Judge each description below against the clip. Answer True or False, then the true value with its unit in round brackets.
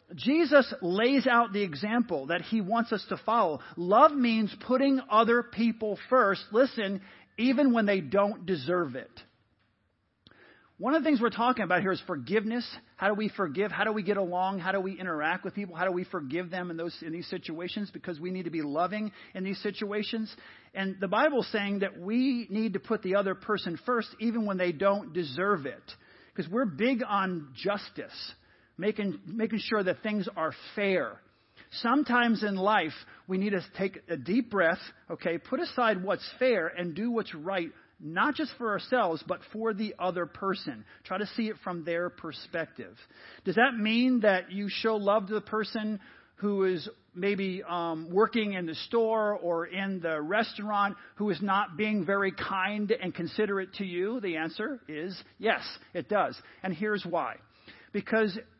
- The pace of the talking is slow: False (180 wpm)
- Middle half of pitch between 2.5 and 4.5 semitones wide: True (3.5 semitones)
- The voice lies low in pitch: False (200 Hz)